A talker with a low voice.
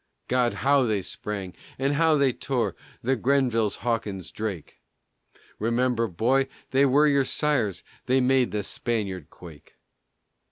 Yes: low, 120 Hz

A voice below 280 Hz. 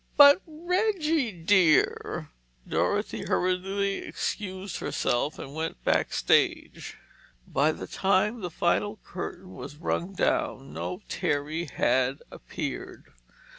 Yes: medium, 185 Hz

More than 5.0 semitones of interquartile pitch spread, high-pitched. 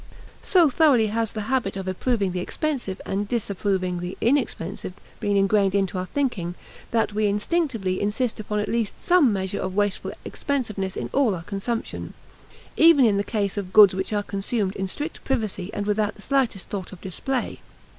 No: average, 3.9 semitones; high, 205 Hz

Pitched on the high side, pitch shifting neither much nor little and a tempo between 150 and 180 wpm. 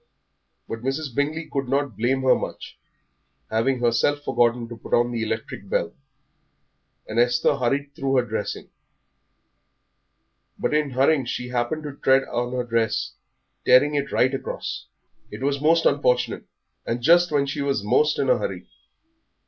No: low, 130 Hz; average, 3.1 semitones; average, 155 wpm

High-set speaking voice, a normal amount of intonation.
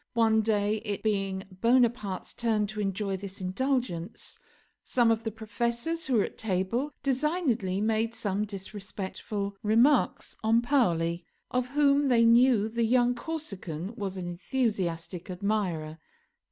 Yes: high, 215 Hz; average, 3.9 semitones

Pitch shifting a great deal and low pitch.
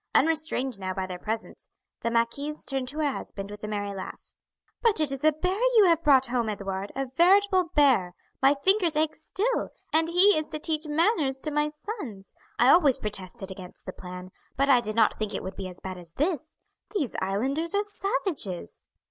No: wide, 7.7 semitones; very high, 270 Hz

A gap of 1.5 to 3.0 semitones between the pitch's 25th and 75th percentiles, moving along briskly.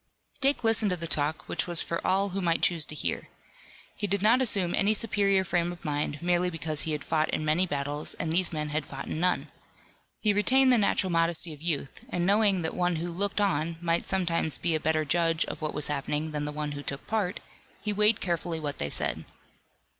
No: average, 4.2 semitones; fast, 220 wpm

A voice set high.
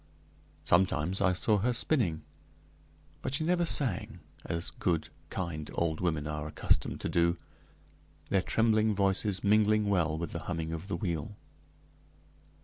No: very low, 90 Hz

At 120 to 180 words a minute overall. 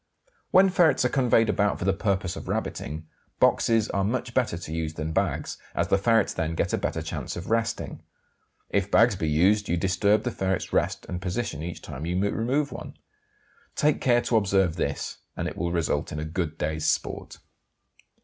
No: average, 190 wpm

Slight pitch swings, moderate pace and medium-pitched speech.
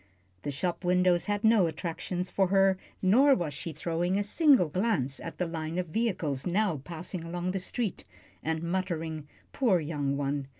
No: average, 3.4 semitones; average, 170 wpm; medium, 175 Hz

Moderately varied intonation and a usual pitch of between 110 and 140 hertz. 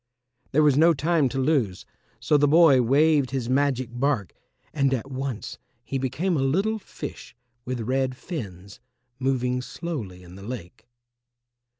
Yes: average, 3.3 semitones; low, 135 Hz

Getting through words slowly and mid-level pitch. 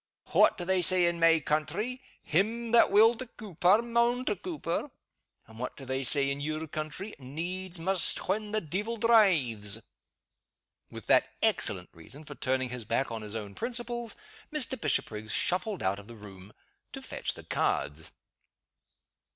No: average, 160 wpm; medium, 170 Hz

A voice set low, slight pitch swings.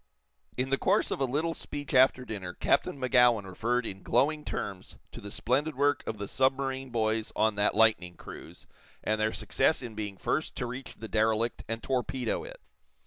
No: low, 120 Hz; average, 3.7 semitones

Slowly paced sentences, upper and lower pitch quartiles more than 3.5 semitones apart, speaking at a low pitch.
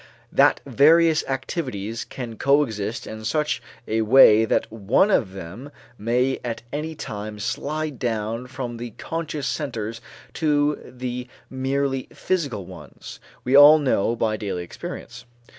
Yes: slow, 130 wpm; average, 4.8 semitones; low, 125 Hz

